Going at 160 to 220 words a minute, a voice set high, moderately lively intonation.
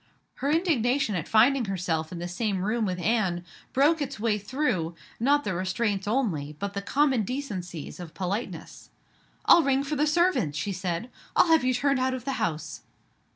No: average, 180 wpm; high, 220 Hz; wide, 7.0 semitones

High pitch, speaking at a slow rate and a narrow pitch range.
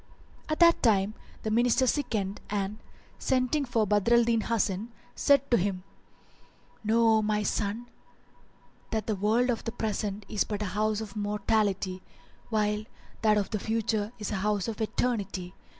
No: high, 215 Hz; average, 160 wpm; narrow, 2.0 semitones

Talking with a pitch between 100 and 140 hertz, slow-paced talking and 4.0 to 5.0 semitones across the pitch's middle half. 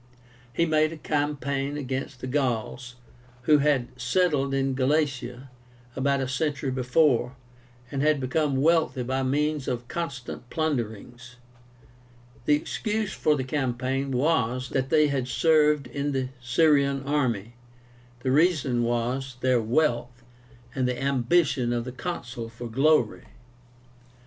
No: low, 135 Hz; slow, 130 wpm; average, 3.2 semitones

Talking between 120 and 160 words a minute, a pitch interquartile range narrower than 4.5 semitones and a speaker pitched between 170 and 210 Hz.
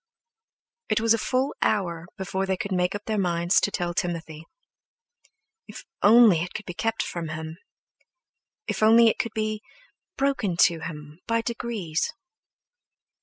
No: average, 150 wpm; average, 4.8 semitones; high, 190 Hz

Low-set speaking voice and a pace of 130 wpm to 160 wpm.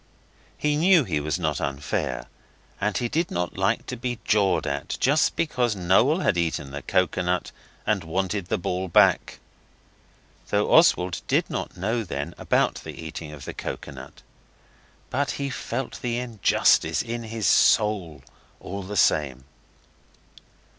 Yes: low, 100 Hz; average, 145 wpm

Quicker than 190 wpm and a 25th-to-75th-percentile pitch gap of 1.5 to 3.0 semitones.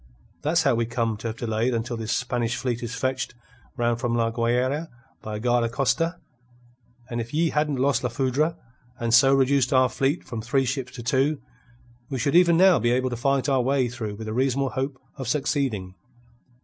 Yes: average, 200 wpm; narrow, 2.6 semitones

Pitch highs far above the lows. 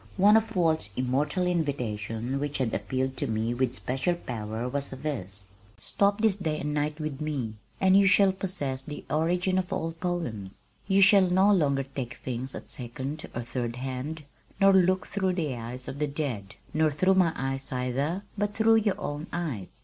Yes: wide, 6.3 semitones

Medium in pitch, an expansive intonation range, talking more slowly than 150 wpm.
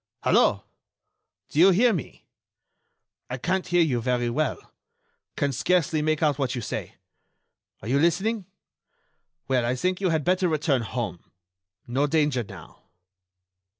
Yes: medium, 150 Hz; wide, 5.9 semitones; average, 140 wpm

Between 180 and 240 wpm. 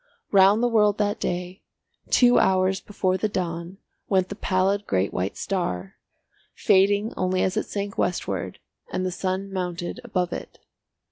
No: average, 150 wpm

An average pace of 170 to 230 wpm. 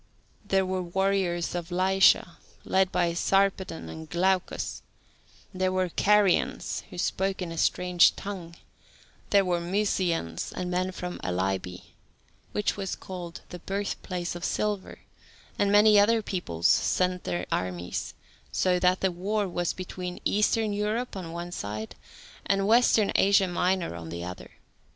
No: average, 140 wpm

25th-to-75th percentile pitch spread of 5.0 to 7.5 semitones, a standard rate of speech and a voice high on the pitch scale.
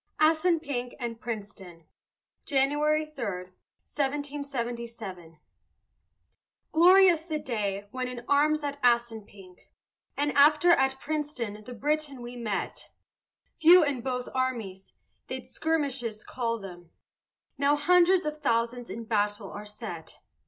No: wide, 5.4 semitones; slow, 110 wpm; very high, 250 Hz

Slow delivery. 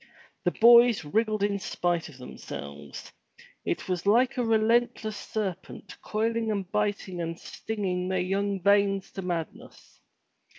Yes: slow, 130 wpm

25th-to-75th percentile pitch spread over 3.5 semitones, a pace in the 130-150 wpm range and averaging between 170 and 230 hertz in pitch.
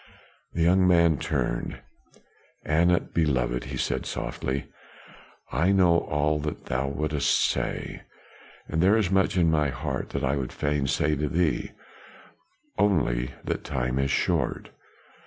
No: average, 4.1 semitones; average, 140 wpm; very low, 75 Hz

